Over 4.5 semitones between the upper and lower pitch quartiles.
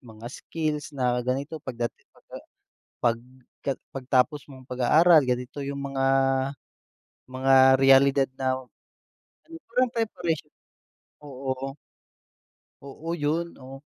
No: narrow, 2.6 semitones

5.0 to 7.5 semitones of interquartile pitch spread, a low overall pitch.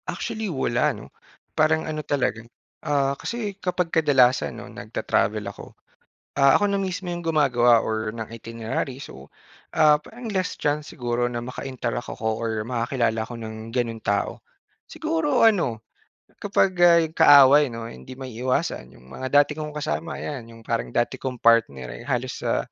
Yes: average, 5.3 semitones; low, 130 Hz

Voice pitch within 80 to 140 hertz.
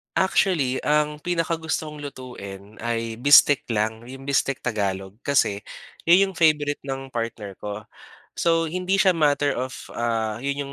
Yes: low, 135 Hz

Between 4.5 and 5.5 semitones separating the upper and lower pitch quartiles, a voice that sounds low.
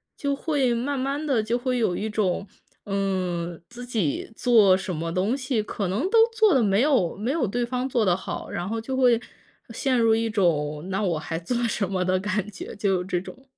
No: average, 5.2 semitones; high, 215 Hz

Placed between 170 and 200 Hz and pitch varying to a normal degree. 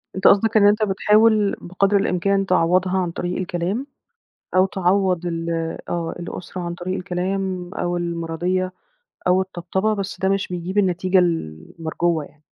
No: medium, 185 Hz; narrow, 2.0 semitones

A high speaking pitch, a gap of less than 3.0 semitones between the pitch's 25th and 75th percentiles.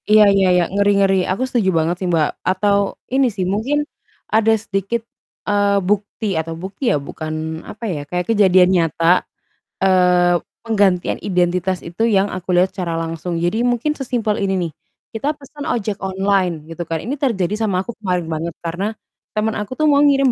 No: high, 195 Hz; average, 3.6 semitones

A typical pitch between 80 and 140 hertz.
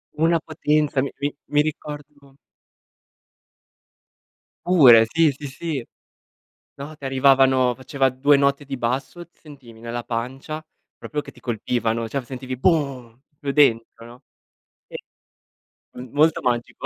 Yes: low, 135 Hz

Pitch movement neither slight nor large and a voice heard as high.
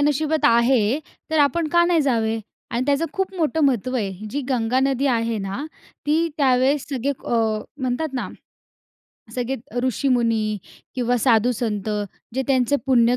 Yes: average, 3.6 semitones; very high, 255 Hz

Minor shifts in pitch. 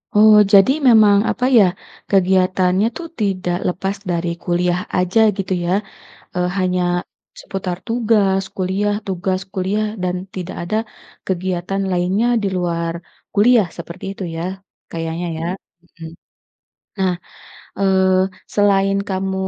Yes: narrow, 1.8 semitones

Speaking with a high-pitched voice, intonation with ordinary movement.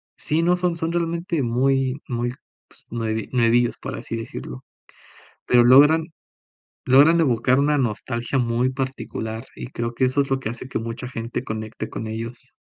No: low, 125 Hz; average, 3.2 semitones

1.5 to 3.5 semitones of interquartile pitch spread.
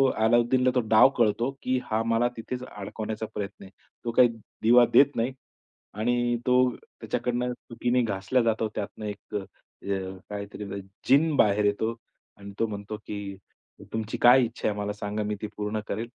Yes: average, 2.9 semitones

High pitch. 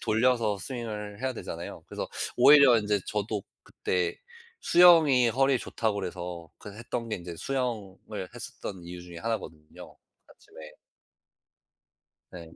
No: low, 105 Hz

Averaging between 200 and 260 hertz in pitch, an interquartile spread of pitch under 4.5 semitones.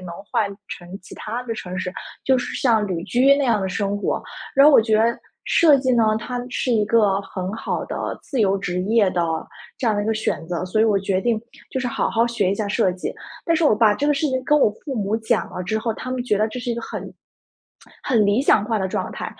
Yes: high, 220 Hz; average, 3.7 semitones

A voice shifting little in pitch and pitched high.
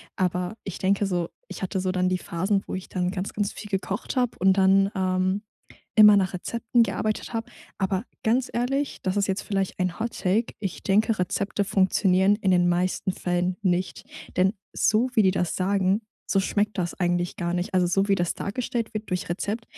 Yes: narrow, 2.3 semitones; high, 195 Hz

